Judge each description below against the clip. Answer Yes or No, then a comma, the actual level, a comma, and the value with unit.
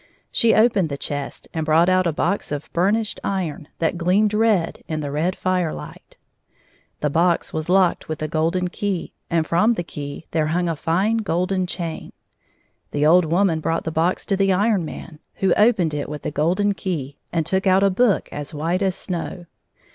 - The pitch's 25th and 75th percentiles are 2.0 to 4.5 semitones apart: Yes, average, 3.4 semitones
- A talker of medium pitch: Yes, medium, 175 Hz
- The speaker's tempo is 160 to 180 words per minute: No, average, 190 wpm